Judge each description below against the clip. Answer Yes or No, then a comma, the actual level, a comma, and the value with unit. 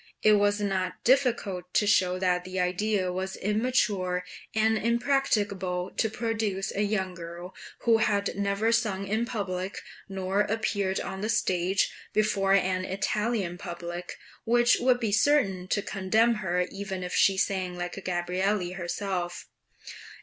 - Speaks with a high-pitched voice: Yes, high, 195 Hz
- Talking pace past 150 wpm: No, average, 140 wpm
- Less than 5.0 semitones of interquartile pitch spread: Yes, average, 2.8 semitones